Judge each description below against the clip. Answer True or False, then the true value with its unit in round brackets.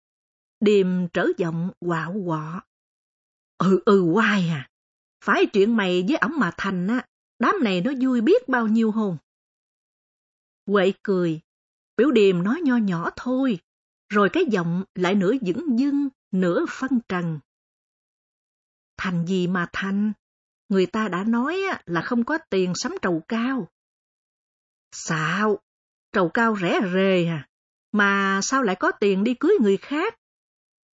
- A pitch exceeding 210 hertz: False (195 Hz)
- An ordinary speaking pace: False (140 wpm)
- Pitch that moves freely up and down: False (4.7 semitones)